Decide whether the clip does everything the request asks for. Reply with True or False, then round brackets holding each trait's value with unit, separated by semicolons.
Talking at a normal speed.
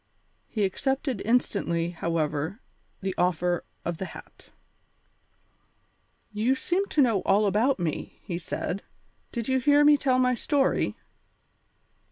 False (125 wpm)